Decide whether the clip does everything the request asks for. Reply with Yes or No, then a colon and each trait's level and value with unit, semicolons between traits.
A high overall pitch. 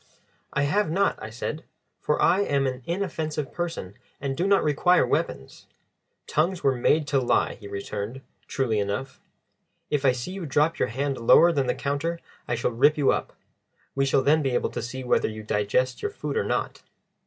No: medium, 140 Hz